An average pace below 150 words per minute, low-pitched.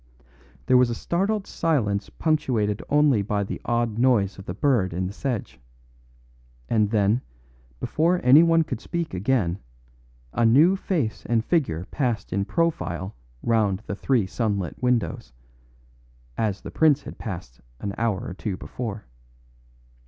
Yes: average, 140 wpm; low, 115 Hz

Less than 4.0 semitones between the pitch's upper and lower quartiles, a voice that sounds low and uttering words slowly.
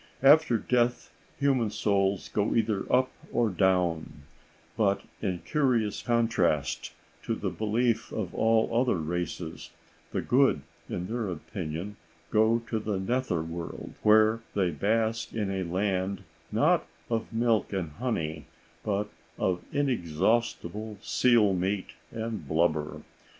No: average, 4.3 semitones; low, 105 Hz; slow, 125 wpm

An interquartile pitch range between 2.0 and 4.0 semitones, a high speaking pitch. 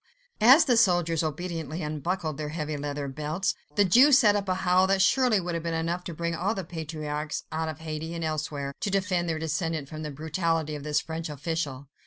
No: average, 3.2 semitones; medium, 165 Hz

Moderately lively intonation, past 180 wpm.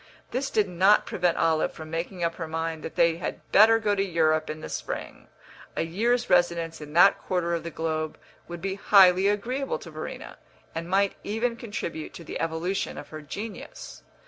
Yes: average, 3.8 semitones; average, 190 wpm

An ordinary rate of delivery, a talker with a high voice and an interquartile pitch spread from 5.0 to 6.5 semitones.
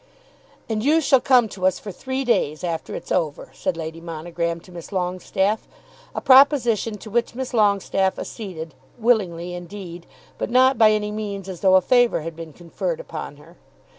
Yes: average, 175 wpm; high, 195 Hz; wide, 5.4 semitones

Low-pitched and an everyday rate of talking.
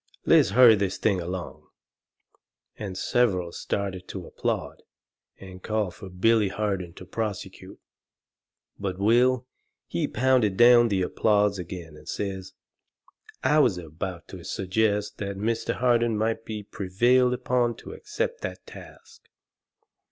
No: low, 105 Hz; slow, 130 wpm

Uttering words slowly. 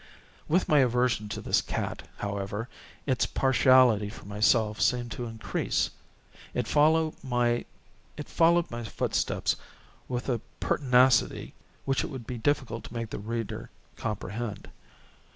Yes: slow, 120 wpm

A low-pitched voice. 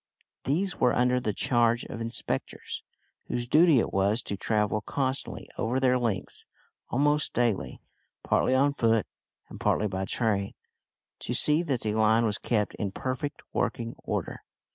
Yes: low, 120 Hz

